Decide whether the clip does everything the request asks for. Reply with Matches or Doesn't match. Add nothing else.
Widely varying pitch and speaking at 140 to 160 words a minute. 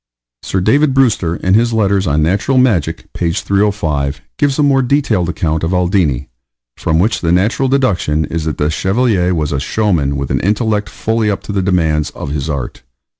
Doesn't match